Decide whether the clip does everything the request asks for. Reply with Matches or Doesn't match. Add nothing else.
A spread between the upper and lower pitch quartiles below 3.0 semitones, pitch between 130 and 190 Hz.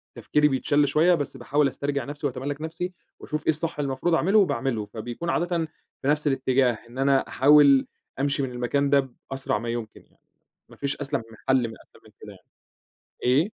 Matches